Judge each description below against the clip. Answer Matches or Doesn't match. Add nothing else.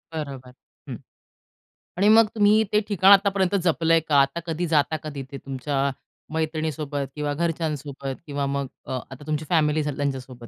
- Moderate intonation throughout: Matches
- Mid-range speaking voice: Matches